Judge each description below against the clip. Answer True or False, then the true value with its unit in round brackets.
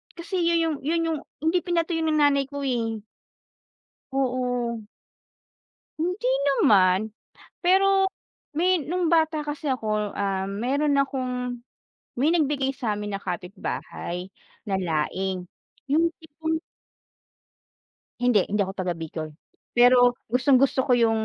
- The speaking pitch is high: True (255 Hz)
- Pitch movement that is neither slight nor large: False (7.2 semitones)